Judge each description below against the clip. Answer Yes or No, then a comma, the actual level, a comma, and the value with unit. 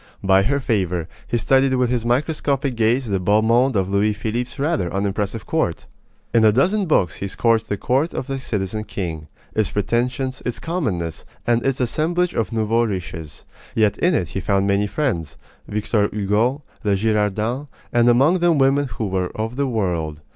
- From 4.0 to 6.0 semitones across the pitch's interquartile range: Yes, average, 5.0 semitones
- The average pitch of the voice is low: Yes, low, 115 Hz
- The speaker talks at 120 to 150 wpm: No, average, 175 wpm